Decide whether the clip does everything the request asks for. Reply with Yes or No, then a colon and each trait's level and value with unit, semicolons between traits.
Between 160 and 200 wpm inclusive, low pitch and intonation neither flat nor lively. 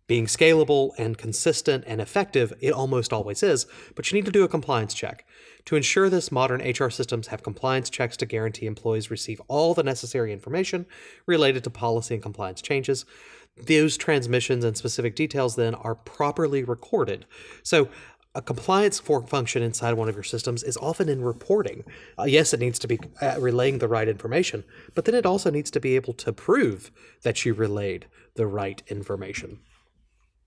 Yes: average, 180 wpm; low, 125 Hz; average, 4.7 semitones